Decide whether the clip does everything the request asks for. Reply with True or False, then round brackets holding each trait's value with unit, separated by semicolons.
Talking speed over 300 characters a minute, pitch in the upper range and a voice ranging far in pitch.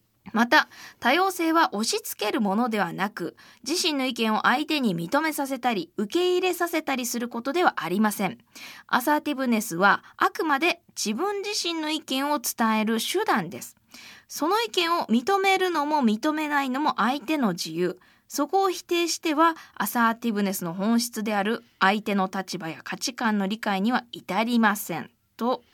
True (330 characters per minute; 250 Hz; 7.4 semitones)